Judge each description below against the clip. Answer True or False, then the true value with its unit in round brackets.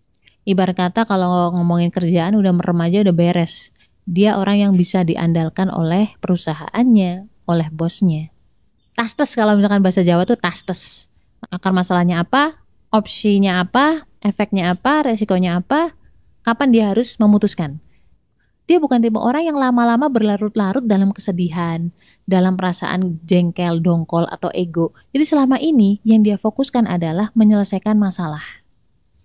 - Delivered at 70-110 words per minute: False (130 wpm)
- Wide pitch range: False (3.9 semitones)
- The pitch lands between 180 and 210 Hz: True (190 Hz)